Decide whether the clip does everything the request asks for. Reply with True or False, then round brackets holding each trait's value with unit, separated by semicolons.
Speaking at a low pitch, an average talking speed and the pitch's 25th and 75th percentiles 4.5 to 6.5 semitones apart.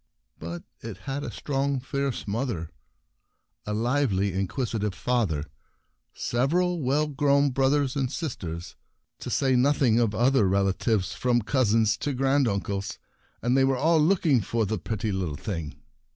True (125 Hz; 145 wpm; 5.4 semitones)